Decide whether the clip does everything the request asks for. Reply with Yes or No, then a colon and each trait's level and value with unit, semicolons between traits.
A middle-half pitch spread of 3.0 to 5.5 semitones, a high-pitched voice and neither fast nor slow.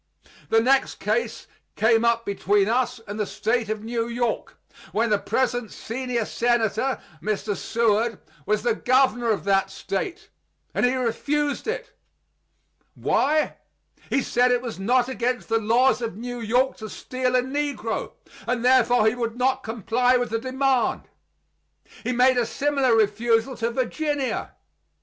No: narrow, 2.5 semitones; high, 240 Hz; average, 150 wpm